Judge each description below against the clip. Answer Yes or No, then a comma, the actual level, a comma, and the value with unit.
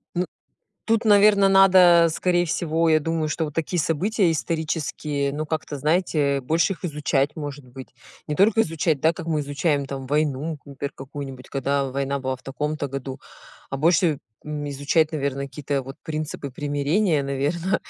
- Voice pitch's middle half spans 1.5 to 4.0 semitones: Yes, average, 3.1 semitones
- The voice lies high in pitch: No, medium, 150 Hz